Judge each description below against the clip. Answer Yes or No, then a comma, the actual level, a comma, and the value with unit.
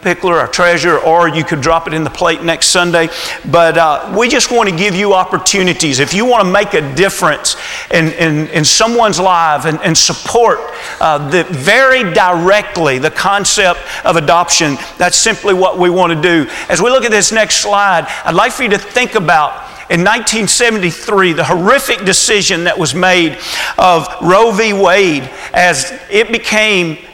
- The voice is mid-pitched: Yes, medium, 180 Hz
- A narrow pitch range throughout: No, average, 3.6 semitones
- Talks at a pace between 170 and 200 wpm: Yes, average, 180 wpm